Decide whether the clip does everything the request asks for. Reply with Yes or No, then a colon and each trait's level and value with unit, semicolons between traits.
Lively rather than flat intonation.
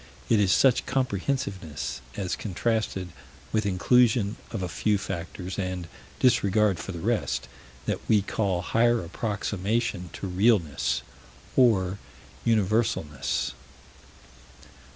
No: average, 3.8 semitones